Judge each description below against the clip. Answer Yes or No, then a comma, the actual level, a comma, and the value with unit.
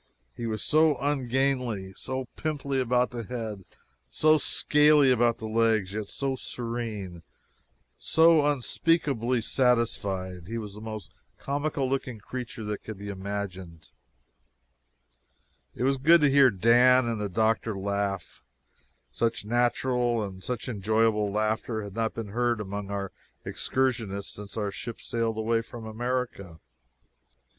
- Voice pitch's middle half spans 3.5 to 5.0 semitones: Yes, average, 3.8 semitones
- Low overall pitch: Yes, low, 115 Hz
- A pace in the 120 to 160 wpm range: Yes, slow, 135 wpm